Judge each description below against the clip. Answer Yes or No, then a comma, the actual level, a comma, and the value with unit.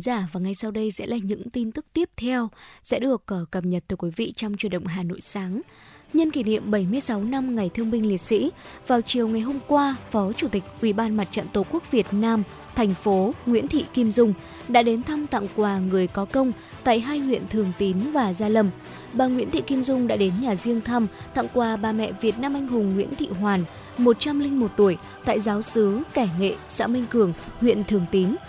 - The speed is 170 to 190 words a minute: No, average, 225 wpm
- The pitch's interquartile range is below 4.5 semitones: Yes, average, 3.8 semitones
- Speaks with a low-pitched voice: No, high, 225 Hz